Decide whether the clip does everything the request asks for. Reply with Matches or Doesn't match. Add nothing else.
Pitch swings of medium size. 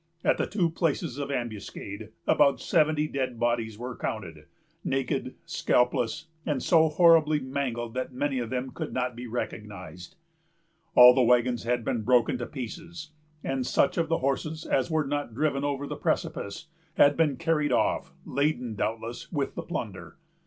Matches